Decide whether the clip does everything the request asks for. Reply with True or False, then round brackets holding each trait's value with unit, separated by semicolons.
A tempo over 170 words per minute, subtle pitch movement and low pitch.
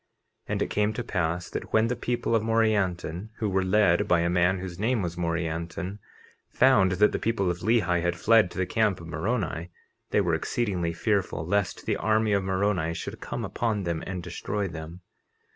False (195 wpm; 3.8 semitones; 95 Hz)